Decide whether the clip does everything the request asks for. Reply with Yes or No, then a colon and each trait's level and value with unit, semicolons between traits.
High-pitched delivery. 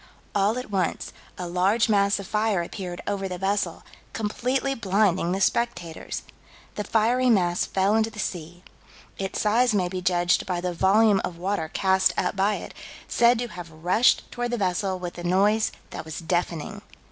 Yes: high, 195 Hz